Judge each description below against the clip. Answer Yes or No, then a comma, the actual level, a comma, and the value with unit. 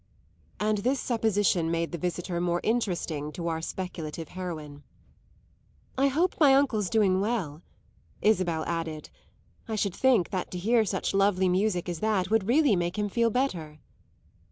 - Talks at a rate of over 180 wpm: No, average, 155 wpm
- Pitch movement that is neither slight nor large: Yes, average, 4.3 semitones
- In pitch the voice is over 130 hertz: Yes, high, 190 Hz